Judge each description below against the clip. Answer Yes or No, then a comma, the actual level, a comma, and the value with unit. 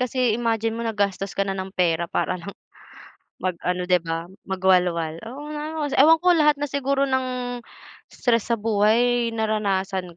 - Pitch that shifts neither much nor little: Yes, average, 4.9 semitones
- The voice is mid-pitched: No, high, 215 Hz